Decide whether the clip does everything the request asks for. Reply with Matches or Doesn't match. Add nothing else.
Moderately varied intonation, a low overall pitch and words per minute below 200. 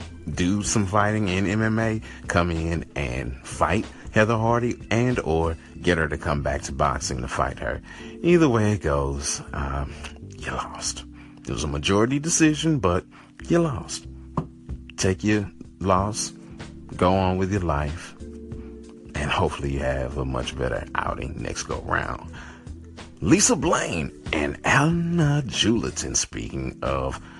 Doesn't match